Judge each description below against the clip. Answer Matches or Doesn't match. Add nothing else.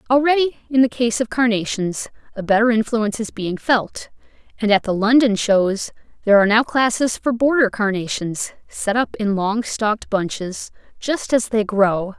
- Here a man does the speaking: Doesn't match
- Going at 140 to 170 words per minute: Matches